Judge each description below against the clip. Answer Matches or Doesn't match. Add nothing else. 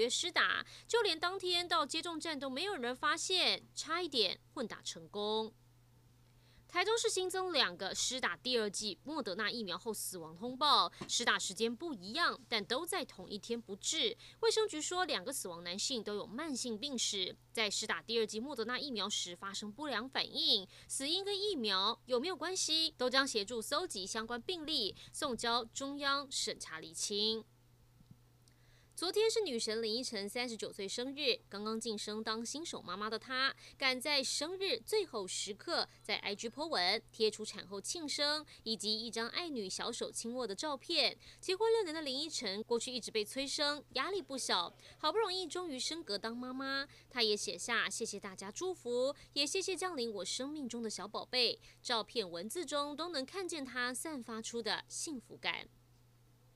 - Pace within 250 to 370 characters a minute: Matches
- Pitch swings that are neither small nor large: Doesn't match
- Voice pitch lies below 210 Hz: Doesn't match